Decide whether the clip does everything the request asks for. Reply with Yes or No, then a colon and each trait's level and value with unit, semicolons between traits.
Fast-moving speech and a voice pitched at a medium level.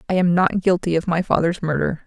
Yes: fast, 235 wpm; medium, 175 Hz